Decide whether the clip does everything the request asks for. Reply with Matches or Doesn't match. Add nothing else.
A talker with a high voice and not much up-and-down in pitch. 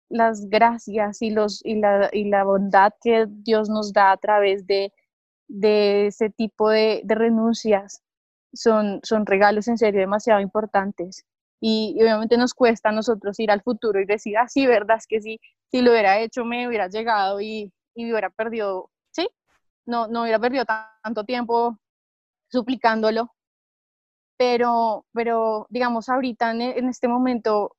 Matches